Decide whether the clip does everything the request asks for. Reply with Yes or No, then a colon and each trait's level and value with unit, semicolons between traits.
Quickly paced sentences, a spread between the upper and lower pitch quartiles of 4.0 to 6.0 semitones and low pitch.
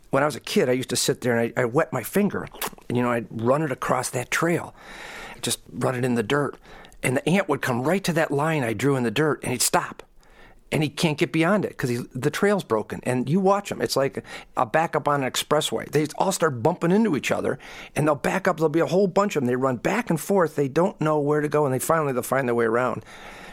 No: fast, 270 wpm; average, 4.9 semitones; medium, 145 Hz